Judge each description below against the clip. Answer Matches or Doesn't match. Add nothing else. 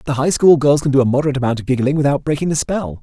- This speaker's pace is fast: Matches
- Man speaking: Matches